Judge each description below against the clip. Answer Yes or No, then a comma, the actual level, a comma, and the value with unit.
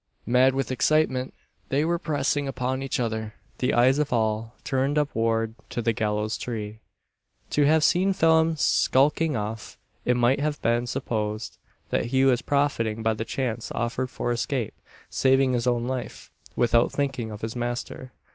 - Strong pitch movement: No, average, 3.4 semitones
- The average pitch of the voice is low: Yes, low, 125 Hz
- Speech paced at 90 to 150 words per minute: No, average, 160 wpm